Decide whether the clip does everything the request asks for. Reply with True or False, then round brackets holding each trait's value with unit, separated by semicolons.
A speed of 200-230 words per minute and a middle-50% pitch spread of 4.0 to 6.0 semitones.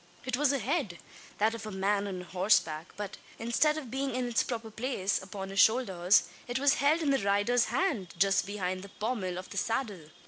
True (205 wpm; 5.0 semitones)